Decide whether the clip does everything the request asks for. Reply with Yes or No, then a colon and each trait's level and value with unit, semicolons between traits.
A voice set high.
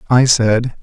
No: low, 120 Hz